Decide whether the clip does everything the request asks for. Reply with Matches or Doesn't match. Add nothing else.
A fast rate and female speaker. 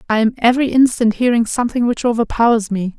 Doesn't match